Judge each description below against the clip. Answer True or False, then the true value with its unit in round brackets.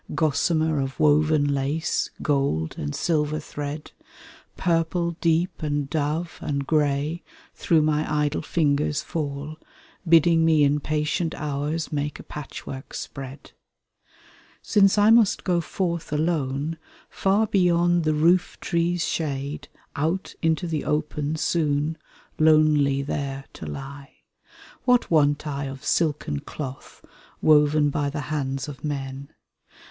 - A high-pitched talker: False (150 Hz)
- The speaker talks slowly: True (120 wpm)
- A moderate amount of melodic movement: False (2.3 semitones)